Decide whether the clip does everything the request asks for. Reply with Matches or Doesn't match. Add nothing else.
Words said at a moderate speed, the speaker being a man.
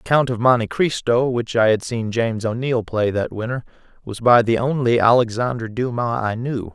Matches